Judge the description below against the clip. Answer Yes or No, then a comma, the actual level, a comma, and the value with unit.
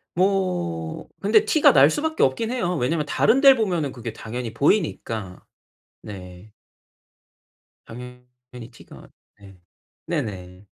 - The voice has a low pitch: Yes, low, 125 Hz